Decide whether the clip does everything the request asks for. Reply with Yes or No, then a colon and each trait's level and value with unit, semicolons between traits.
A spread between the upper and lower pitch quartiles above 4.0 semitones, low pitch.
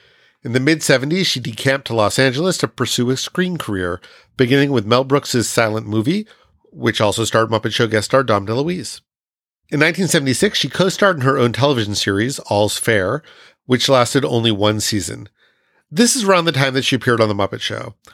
Yes: average, 4.7 semitones; low, 125 Hz